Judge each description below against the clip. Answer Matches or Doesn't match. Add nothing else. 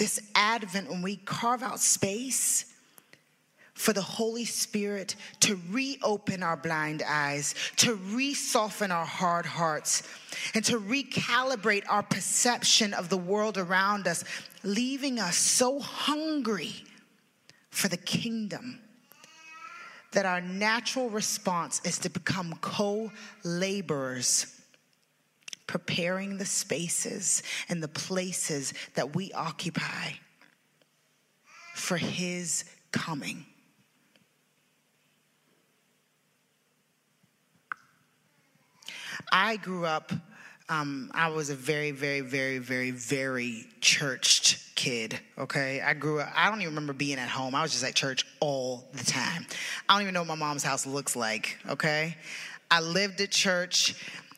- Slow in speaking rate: Matches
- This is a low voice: Doesn't match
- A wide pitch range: Matches